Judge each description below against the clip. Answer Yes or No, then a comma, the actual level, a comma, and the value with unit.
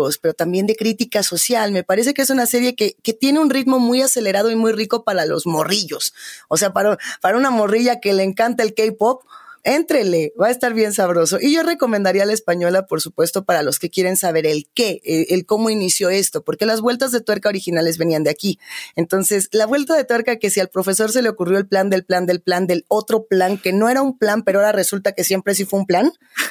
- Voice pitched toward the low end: No, high, 210 Hz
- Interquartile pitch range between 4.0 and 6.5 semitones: Yes, average, 4.5 semitones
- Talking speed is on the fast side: Yes, fast, 240 wpm